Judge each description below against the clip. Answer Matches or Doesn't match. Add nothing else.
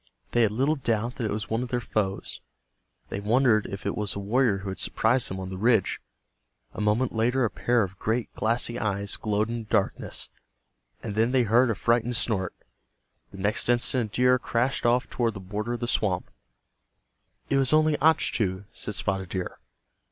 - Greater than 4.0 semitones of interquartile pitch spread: Doesn't match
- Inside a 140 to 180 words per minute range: Doesn't match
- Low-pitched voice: Matches